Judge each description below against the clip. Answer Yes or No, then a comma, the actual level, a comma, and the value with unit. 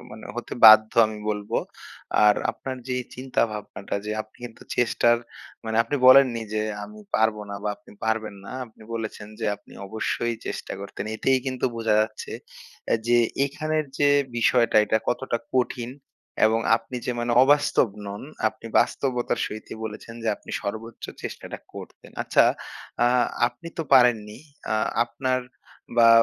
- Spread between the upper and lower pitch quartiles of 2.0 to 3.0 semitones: Yes, narrow, 2.6 semitones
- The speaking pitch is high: No, low, 115 Hz